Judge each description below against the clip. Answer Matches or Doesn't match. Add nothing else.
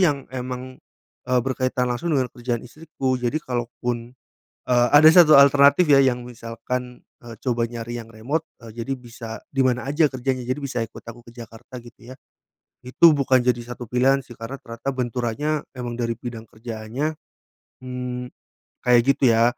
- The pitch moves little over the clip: Matches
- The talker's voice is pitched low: Matches